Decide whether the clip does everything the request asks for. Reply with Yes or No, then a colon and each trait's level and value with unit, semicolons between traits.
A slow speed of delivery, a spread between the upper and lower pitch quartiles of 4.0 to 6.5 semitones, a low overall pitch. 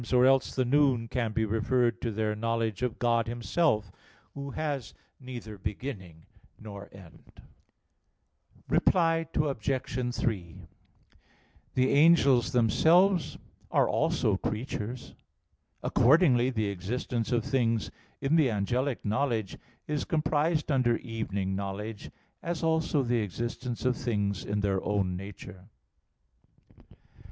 Yes: slow, 115 wpm; average, 4.5 semitones; low, 120 Hz